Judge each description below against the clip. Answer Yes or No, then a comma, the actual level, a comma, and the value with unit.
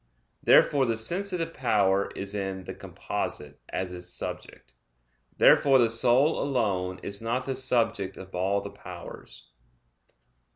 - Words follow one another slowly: Yes, slow, 130 wpm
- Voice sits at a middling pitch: No, low, 110 Hz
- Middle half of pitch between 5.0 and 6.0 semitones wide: Yes, wide, 5.4 semitones